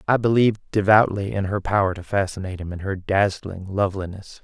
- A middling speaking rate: Yes, average, 175 wpm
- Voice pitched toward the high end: No, low, 100 Hz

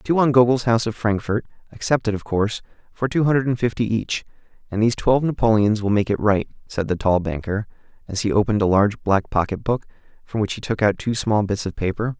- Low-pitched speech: Yes, low, 110 Hz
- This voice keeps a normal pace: No, fast, 210 wpm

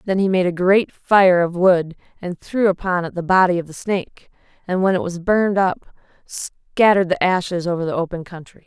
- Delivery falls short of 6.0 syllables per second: Yes, 5.1 syllables/s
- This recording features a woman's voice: Yes, female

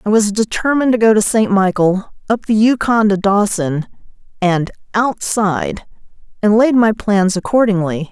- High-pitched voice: Yes, high, 210 Hz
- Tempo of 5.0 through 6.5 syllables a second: No, 4.8 syllables/s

